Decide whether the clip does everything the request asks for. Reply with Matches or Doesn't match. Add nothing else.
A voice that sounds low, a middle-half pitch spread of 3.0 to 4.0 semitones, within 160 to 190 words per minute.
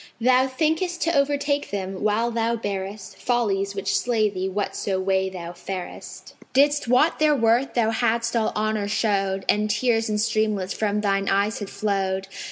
Doesn't match